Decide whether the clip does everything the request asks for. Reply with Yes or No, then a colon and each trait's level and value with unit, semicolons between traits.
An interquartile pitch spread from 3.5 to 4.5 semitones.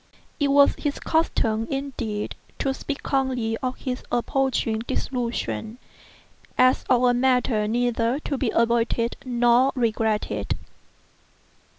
No: average, 2.7 semitones